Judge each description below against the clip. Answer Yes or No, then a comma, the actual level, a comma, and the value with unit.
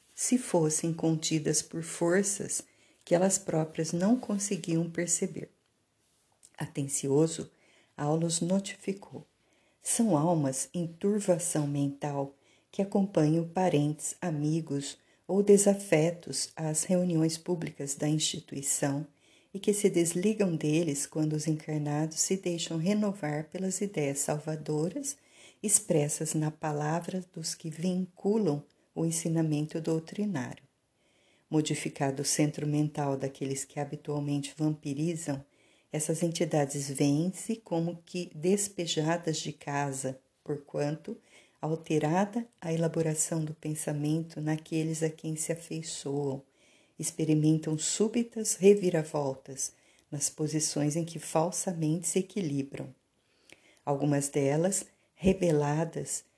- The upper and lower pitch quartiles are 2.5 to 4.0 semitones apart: Yes, average, 3.1 semitones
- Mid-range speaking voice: Yes, medium, 160 Hz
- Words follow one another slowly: Yes, slow, 100 wpm